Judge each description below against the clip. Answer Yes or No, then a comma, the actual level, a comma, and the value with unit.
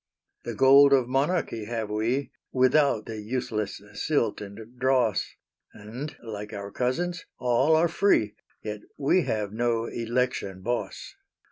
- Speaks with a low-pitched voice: Yes, low, 120 Hz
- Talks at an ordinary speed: No, slow, 130 wpm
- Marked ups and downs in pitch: No, average, 4.1 semitones